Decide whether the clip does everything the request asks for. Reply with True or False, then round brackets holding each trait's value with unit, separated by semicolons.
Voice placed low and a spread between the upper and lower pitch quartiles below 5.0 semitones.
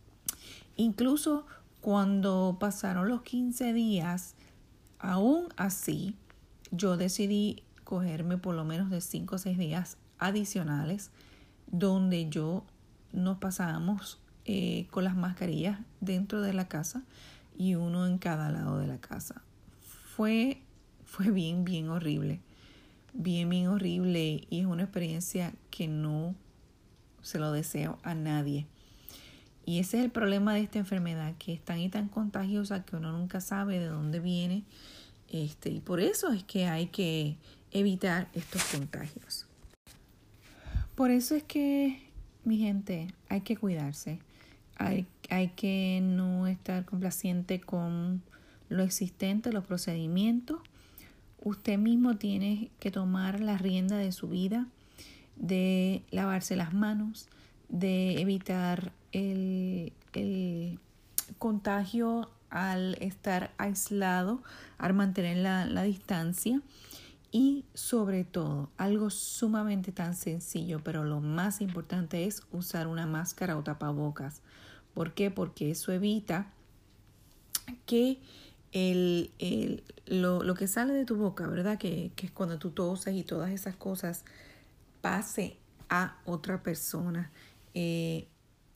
False (185 Hz; 2.9 semitones)